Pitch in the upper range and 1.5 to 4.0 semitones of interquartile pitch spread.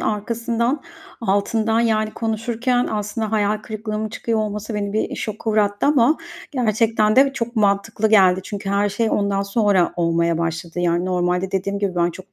Yes: high, 210 Hz; narrow, 2.4 semitones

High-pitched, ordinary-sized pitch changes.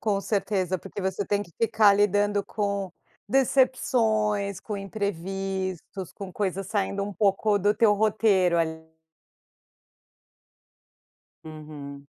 No: high, 200 Hz; narrow, 1.9 semitones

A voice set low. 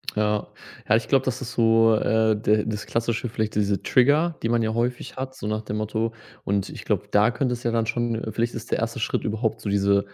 Yes: low, 115 Hz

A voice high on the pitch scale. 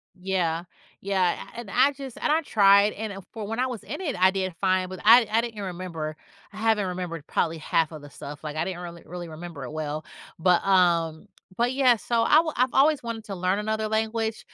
Yes: high, 195 Hz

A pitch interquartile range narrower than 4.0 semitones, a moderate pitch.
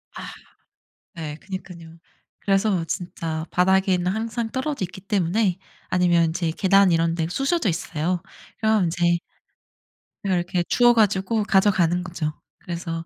Yes: average, 2.9 semitones; medium, 180 Hz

